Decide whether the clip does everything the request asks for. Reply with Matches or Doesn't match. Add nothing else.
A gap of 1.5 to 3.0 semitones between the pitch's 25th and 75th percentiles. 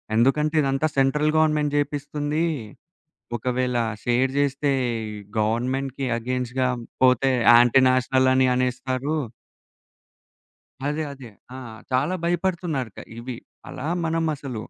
Matches